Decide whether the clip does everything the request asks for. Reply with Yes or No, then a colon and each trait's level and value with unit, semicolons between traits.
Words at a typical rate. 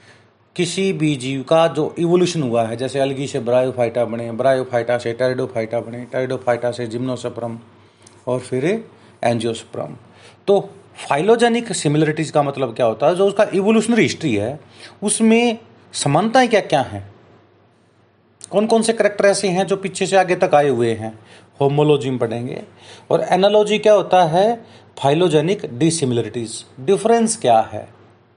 Yes: average, 140 wpm